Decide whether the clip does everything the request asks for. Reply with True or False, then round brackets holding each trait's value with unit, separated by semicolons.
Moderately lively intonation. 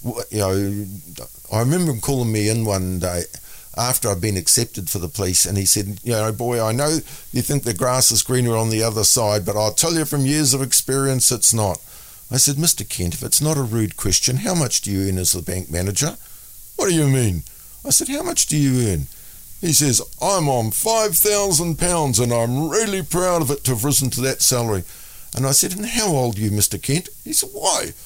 False (5.9 semitones)